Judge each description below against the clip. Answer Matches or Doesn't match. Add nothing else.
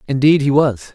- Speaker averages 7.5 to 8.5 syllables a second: Doesn't match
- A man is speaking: Matches